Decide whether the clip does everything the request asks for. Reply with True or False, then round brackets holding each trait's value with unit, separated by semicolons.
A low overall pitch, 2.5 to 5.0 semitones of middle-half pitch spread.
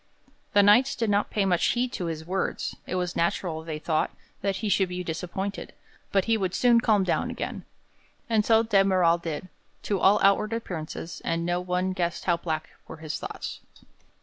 False (185 Hz; 3.3 semitones)